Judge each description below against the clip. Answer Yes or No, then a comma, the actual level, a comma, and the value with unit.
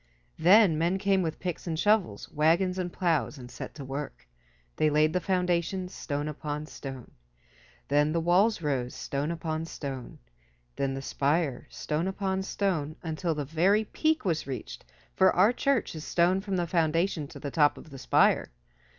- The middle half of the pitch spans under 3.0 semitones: No, average, 4.0 semitones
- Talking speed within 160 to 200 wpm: Yes, average, 170 wpm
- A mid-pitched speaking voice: Yes, medium, 165 Hz